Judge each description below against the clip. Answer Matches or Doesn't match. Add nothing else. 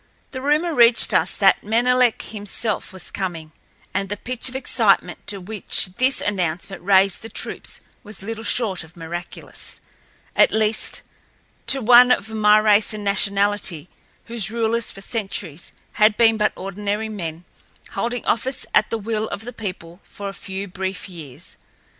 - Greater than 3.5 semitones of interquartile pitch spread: Doesn't match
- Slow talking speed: Doesn't match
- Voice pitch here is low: Doesn't match